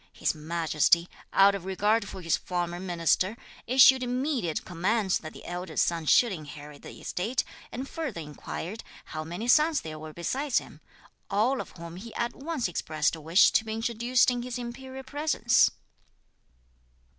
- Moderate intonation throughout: No, wide, 6.6 semitones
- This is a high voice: Yes, high, 200 Hz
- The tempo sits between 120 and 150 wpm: No, average, 160 wpm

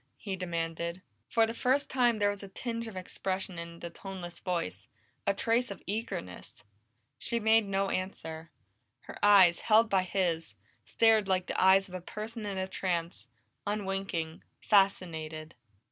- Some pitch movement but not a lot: Yes, average, 3.8 semitones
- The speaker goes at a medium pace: Yes, average, 155 wpm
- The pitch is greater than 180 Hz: Yes, high, 190 Hz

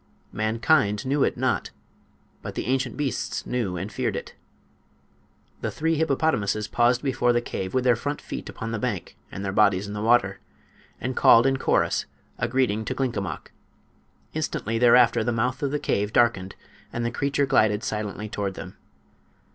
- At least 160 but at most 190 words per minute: Yes, average, 170 wpm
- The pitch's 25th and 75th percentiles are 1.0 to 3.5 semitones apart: No, average, 4.0 semitones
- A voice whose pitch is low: Yes, low, 120 Hz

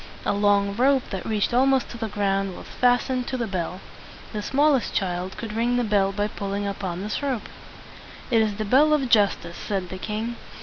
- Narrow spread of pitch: No, average, 3.8 semitones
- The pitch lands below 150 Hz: No, high, 210 Hz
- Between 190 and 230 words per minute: Yes, fast, 205 wpm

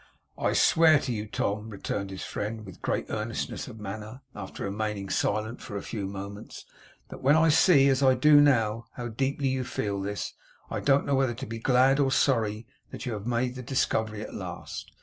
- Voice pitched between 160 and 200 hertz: No, low, 115 Hz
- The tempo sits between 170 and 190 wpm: No, average, 200 wpm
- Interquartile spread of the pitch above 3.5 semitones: Yes, average, 4.2 semitones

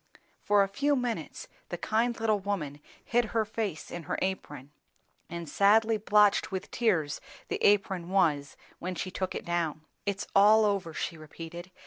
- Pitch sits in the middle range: No, high, 195 Hz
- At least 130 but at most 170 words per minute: Yes, average, 160 wpm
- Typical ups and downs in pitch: Yes, average, 4.2 semitones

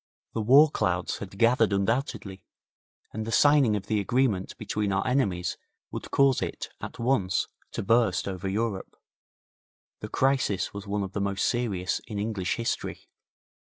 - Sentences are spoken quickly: No, average, 155 wpm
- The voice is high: No, low, 105 Hz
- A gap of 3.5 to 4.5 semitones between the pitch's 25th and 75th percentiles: Yes, average, 3.8 semitones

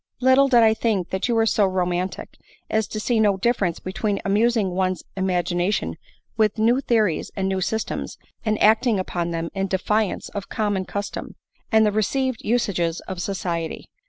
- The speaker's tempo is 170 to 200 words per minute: Yes, average, 175 wpm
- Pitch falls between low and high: No, high, 205 Hz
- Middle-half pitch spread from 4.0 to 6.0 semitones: No, average, 3.0 semitones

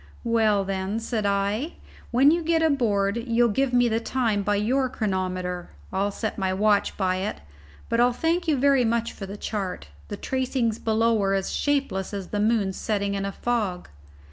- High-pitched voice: Yes, high, 220 Hz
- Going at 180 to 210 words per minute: Yes, average, 190 wpm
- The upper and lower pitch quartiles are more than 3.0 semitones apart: Yes, average, 3.7 semitones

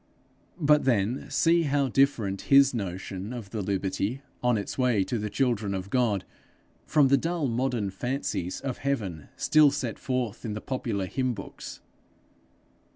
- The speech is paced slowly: No, average, 155 wpm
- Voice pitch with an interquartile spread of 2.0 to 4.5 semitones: No, average, 5.3 semitones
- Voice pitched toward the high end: No, low, 120 Hz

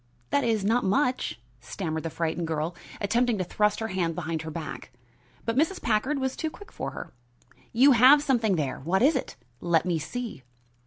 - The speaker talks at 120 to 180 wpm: No, average, 190 wpm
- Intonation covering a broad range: Yes, wide, 7.2 semitones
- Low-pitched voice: No, high, 210 Hz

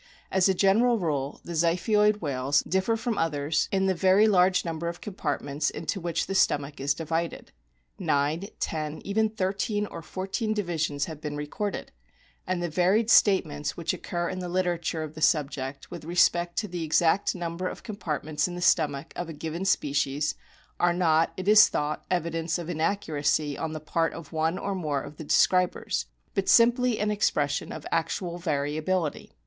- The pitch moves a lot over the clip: No, average, 3.8 semitones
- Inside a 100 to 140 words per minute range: No, average, 175 wpm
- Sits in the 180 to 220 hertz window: No, medium, 170 Hz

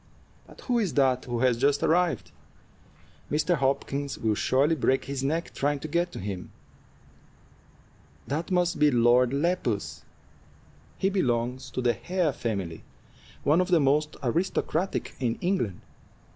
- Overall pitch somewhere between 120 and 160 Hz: Yes, medium, 140 Hz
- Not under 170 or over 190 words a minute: No, average, 140 wpm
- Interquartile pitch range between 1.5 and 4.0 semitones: No, wide, 5.6 semitones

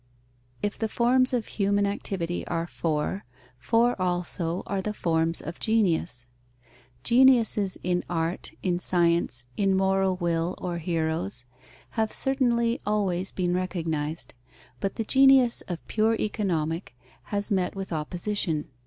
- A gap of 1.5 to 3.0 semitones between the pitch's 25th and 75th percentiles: No, average, 4.2 semitones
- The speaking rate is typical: No, slow, 130 wpm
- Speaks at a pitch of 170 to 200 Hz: Yes, medium, 185 Hz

